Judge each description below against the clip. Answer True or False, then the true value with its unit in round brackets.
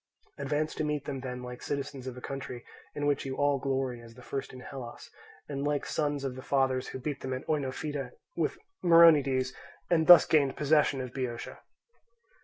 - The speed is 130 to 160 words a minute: False (190 wpm)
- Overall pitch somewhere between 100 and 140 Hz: True (135 Hz)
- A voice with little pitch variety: True (2.3 semitones)